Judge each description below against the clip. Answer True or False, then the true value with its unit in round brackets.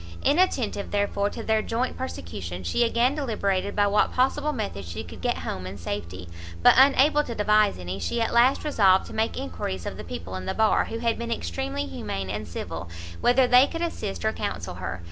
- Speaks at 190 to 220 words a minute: True (200 wpm)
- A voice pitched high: True (205 Hz)